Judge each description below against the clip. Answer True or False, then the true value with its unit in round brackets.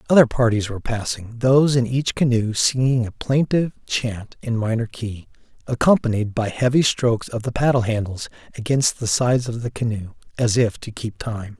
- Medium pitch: False (120 Hz)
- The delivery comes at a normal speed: True (175 wpm)